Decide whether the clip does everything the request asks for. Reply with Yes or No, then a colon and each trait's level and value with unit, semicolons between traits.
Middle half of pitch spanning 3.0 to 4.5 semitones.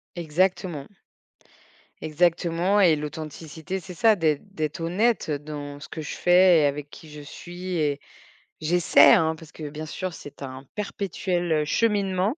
Yes: average, 3.4 semitones